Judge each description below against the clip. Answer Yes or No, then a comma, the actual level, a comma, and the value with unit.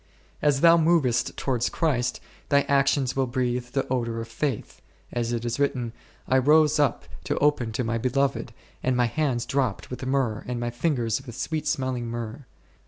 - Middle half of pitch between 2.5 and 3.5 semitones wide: Yes, average, 2.9 semitones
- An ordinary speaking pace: Yes, average, 175 wpm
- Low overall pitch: Yes, low, 130 Hz